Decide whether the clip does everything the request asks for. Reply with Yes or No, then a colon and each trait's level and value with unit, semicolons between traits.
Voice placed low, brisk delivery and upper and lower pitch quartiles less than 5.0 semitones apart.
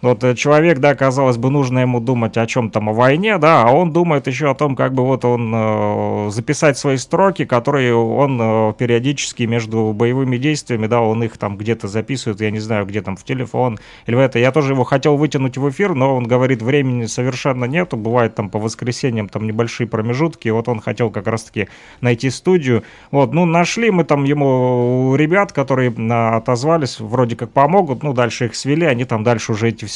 Yes: low, 125 Hz; fast, 200 wpm; average, 3.7 semitones